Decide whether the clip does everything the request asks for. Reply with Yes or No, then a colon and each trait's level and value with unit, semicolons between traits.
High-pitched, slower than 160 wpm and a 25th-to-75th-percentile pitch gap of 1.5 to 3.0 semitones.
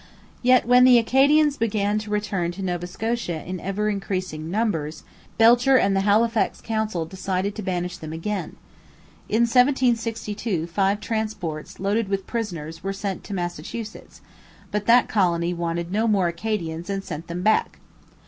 No: high, 200 Hz; average, 150 wpm; average, 4.3 semitones